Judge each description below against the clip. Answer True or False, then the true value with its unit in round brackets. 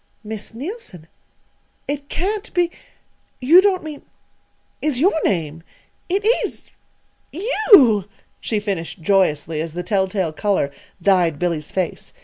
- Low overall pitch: False (205 Hz)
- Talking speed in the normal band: False (120 wpm)